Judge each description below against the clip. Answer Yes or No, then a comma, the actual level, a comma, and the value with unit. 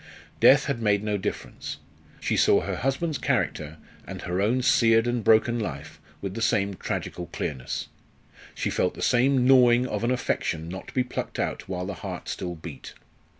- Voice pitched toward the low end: Yes, low, 110 Hz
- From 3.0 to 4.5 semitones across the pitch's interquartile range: No, average, 5.3 semitones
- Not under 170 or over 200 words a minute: Yes, average, 180 wpm